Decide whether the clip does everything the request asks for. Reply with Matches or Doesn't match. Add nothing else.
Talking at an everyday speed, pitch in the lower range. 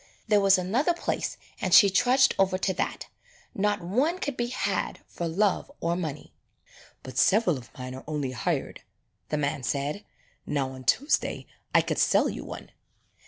Doesn't match